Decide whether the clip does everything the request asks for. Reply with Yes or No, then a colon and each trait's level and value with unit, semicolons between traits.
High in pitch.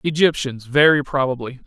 No: medium, 140 Hz